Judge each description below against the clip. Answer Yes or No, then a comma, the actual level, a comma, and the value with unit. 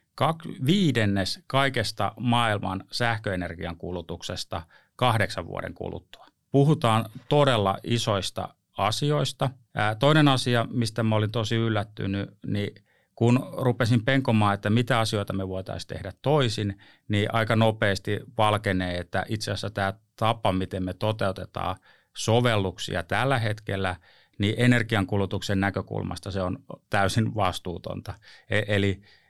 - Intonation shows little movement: No, average, 3.5 semitones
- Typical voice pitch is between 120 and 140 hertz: No, low, 105 Hz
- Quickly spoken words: No, average, 115 wpm